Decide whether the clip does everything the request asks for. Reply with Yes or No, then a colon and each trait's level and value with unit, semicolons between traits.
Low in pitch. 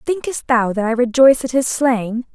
No: very high, 250 Hz